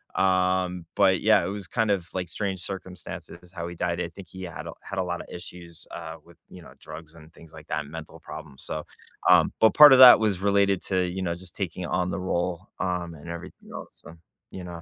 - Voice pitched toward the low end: Yes, very low, 90 Hz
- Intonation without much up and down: Yes, narrow, 2.0 semitones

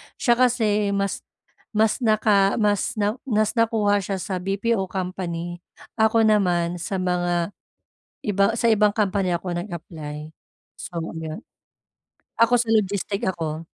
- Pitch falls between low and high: No, high, 200 Hz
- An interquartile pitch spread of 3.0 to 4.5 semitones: Yes, average, 3.5 semitones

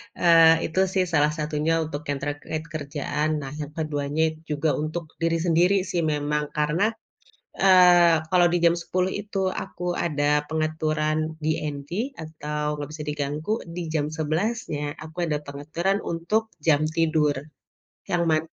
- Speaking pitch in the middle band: Yes, medium, 155 Hz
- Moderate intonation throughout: No, narrow, 2.3 semitones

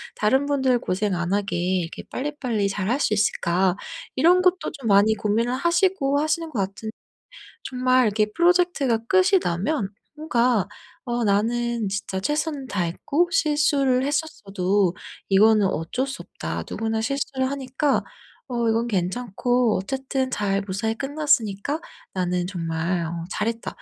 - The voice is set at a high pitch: Yes, high, 235 Hz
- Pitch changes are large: Yes, wide, 5.9 semitones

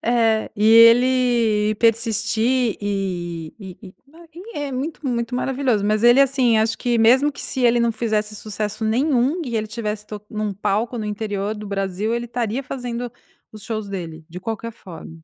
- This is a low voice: No, high, 225 Hz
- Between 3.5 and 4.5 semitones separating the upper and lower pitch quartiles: No, average, 2.7 semitones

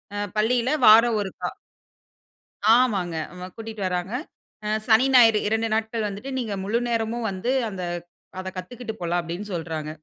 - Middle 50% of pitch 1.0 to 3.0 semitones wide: No, average, 3.7 semitones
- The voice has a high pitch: Yes, high, 220 Hz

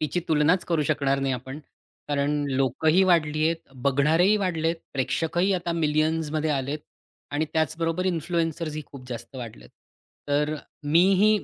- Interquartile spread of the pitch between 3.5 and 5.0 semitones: No, average, 2.8 semitones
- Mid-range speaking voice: Yes, medium, 155 Hz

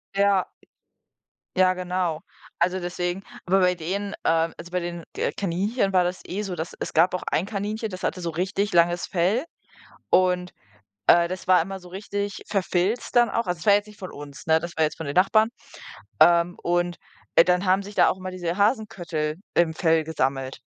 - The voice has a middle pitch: Yes, medium, 180 Hz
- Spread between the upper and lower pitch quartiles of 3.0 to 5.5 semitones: No, narrow, 2.4 semitones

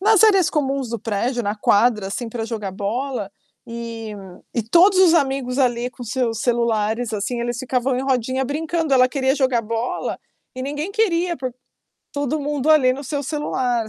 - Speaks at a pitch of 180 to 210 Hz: No, very high, 255 Hz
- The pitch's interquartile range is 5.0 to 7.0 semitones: No, average, 3.7 semitones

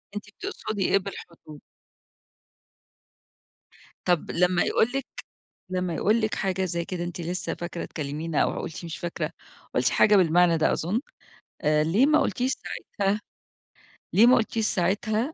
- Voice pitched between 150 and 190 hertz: Yes, medium, 185 Hz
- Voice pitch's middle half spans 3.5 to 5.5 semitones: Yes, average, 4.1 semitones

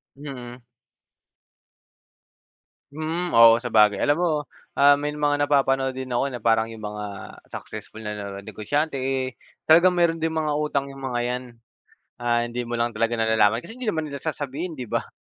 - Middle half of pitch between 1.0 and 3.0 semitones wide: No, average, 4.3 semitones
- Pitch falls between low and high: No, low, 130 Hz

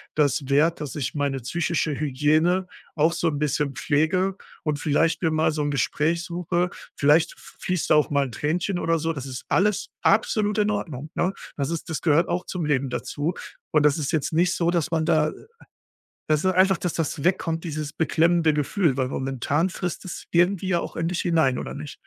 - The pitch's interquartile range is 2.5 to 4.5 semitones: Yes, average, 2.9 semitones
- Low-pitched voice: No, medium, 160 Hz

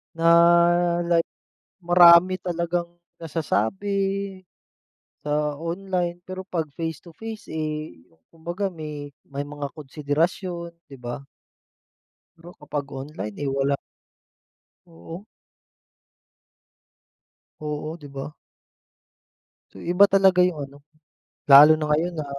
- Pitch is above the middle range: No, medium, 165 Hz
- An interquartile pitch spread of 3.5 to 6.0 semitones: No, average, 2.9 semitones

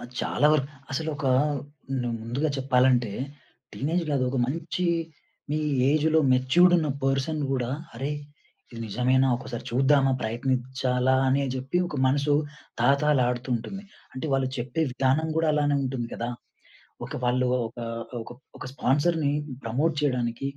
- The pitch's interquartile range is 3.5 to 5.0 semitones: No, average, 2.9 semitones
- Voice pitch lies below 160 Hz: Yes, low, 135 Hz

